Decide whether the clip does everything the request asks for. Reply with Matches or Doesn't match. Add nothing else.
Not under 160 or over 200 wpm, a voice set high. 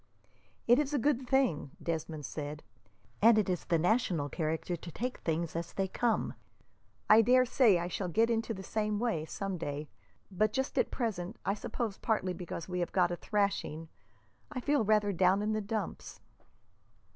Matches